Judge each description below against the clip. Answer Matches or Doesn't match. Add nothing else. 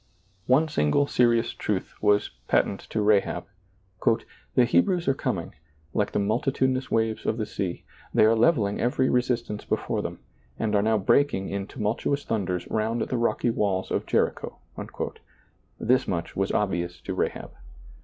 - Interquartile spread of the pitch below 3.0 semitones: Doesn't match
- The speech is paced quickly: Doesn't match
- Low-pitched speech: Matches